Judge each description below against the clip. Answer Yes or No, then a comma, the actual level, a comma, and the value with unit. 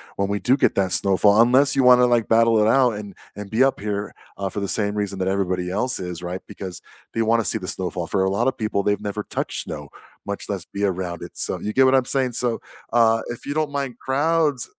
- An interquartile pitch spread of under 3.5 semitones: No, average, 4.2 semitones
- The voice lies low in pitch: Yes, low, 105 Hz